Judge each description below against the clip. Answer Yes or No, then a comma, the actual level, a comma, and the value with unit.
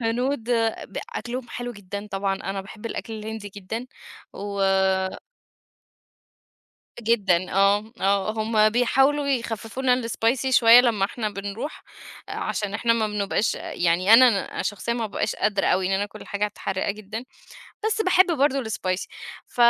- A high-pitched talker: Yes, high, 215 Hz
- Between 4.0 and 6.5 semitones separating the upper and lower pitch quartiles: No, average, 3.2 semitones